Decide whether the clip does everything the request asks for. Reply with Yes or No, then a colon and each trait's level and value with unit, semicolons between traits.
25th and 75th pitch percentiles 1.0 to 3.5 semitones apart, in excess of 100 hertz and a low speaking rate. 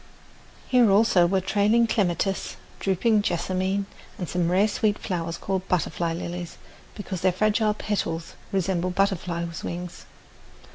Yes: average, 3.0 semitones; high, 190 Hz; slow, 125 wpm